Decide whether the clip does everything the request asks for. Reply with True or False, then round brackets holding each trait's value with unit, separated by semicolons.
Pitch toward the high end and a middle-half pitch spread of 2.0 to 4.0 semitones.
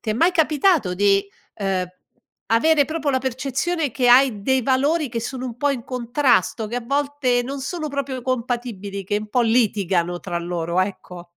False (245 Hz; 5.4 semitones)